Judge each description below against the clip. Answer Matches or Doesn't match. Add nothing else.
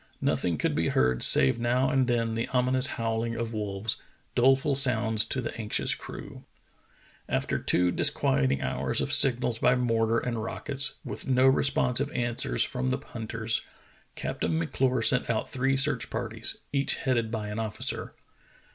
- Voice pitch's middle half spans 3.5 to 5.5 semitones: Doesn't match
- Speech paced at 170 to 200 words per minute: Doesn't match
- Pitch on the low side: Matches